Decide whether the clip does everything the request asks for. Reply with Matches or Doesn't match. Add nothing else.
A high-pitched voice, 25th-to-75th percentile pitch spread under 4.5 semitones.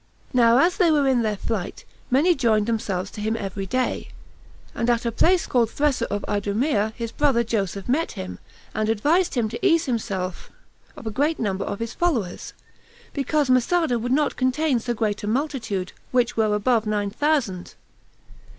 Doesn't match